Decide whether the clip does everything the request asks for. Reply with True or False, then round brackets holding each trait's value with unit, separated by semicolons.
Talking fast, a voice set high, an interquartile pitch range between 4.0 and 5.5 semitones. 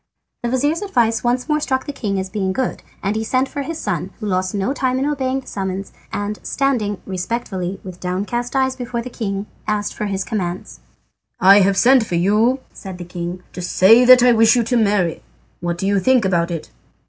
True (210 wpm; 210 Hz; 5.0 semitones)